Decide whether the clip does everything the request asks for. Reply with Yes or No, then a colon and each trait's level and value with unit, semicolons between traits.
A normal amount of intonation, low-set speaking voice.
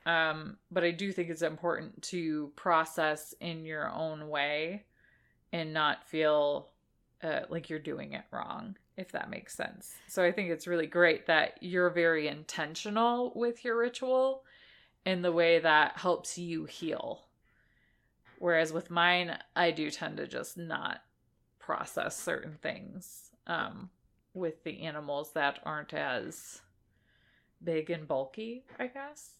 No: average, 3.0 semitones; medium, 170 Hz